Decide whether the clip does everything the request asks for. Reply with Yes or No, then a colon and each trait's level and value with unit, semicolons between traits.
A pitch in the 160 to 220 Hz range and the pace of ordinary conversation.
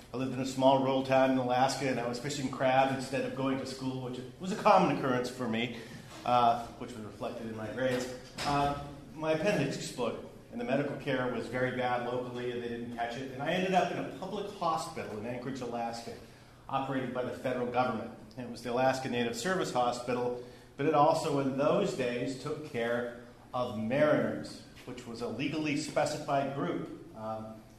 No: low, 125 Hz; average, 195 wpm